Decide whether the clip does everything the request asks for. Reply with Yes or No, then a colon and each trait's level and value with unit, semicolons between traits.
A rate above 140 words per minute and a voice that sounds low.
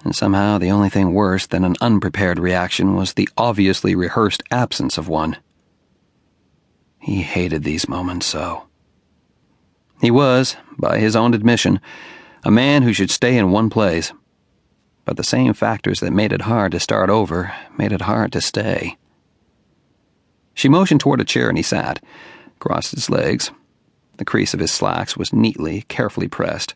Yes: average, 160 wpm; low, 100 Hz